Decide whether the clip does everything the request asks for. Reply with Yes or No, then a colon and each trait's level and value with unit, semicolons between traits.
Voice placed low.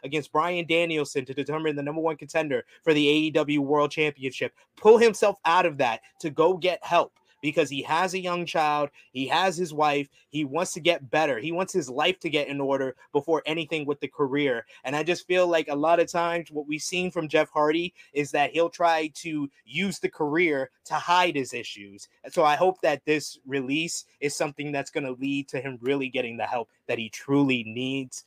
No: medium, 150 Hz